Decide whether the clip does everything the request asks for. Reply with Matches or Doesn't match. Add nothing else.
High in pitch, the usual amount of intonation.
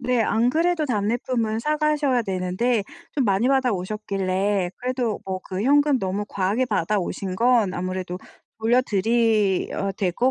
Matches